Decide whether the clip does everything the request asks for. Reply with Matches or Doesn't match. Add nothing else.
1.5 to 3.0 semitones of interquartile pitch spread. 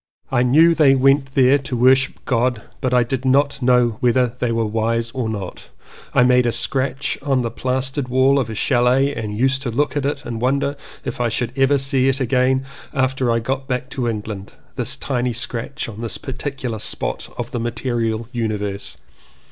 Matches